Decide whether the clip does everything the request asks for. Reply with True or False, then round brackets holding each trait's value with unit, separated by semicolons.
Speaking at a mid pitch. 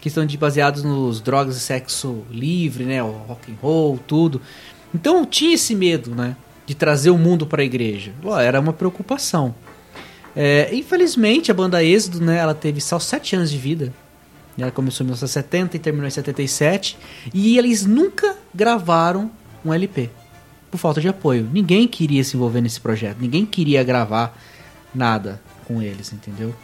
True (145 Hz)